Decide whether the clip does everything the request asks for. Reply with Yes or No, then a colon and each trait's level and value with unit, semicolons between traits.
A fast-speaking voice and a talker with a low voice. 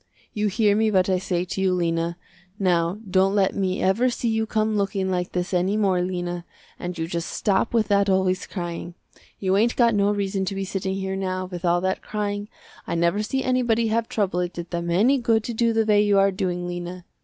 No: fast, 225 wpm; high, 190 Hz